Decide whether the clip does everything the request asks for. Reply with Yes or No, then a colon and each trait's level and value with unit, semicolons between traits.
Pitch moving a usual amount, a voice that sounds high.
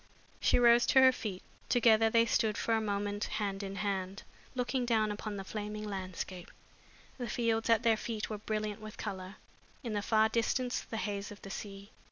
No: narrow, 2.2 semitones; high, 215 Hz